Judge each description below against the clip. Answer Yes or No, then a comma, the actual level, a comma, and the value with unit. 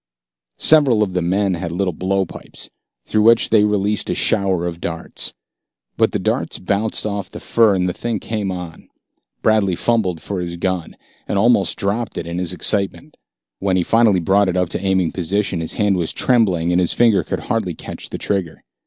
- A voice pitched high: No, very low, 95 Hz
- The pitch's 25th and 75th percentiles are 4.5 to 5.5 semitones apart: No, average, 2.9 semitones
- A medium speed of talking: Yes, average, 190 wpm